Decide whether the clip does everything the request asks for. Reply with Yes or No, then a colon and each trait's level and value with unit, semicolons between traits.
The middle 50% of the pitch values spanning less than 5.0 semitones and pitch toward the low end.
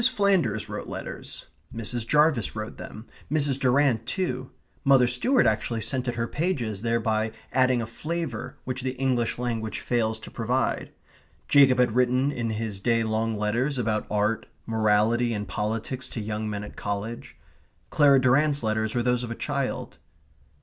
Yes: average, 3.0 semitones; low, 120 Hz